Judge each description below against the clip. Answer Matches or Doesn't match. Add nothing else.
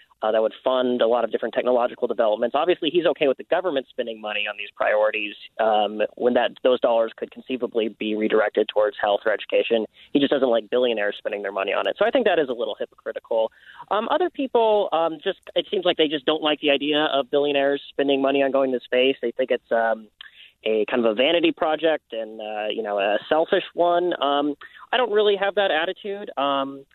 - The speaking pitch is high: Doesn't match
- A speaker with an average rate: Doesn't match